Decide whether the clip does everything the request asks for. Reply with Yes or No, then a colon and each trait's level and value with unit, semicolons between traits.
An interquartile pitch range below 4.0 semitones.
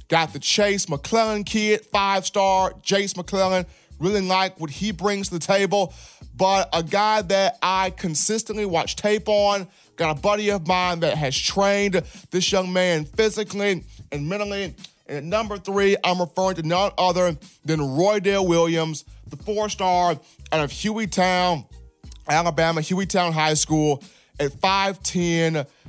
Yes: average, 3.5 semitones